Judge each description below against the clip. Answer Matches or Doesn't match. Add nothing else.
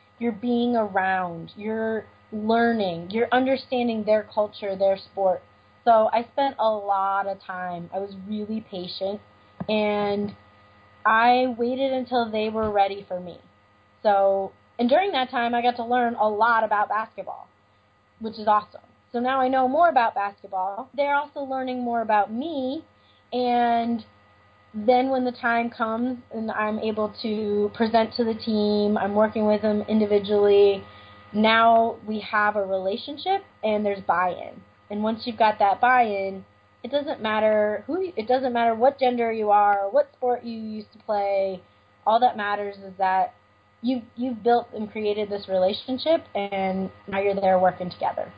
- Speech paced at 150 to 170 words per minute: Matches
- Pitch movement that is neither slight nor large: Matches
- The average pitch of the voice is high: Matches